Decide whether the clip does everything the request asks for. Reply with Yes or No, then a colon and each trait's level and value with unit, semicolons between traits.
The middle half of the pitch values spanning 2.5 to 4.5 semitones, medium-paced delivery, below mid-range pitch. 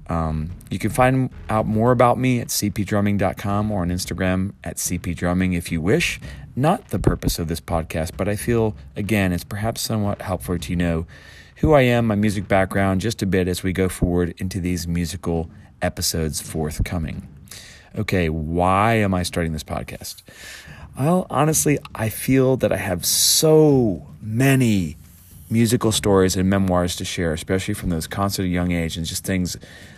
Yes: average, 3.8 semitones; average, 165 wpm; very low, 95 Hz